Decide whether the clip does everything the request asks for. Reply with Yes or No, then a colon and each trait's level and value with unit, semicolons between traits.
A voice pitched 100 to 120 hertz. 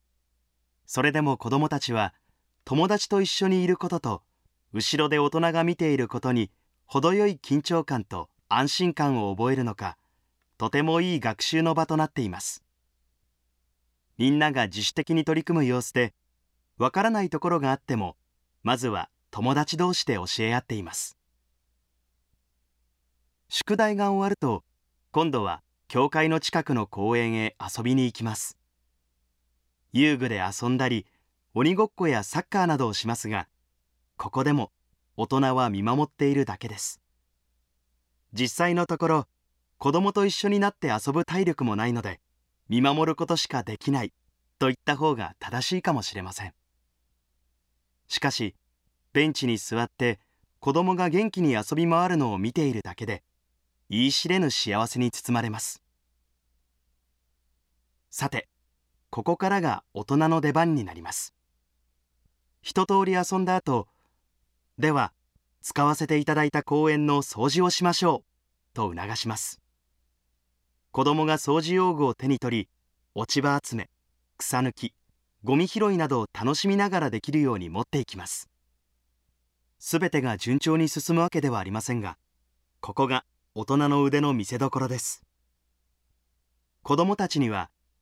Yes: low, 115 Hz